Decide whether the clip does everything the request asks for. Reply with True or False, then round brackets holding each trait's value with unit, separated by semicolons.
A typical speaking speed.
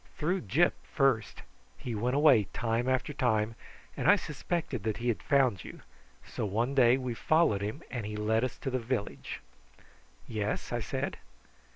True (170 wpm)